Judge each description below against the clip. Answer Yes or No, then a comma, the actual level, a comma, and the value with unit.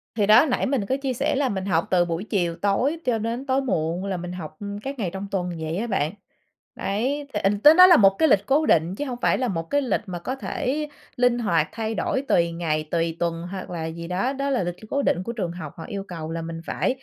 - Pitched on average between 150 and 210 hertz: Yes, high, 195 Hz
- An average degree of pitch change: No, wide, 6.8 semitones